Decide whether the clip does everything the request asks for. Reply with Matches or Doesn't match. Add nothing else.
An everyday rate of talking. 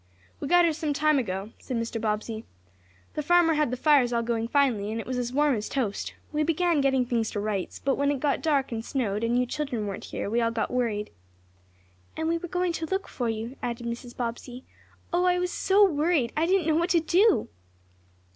Doesn't match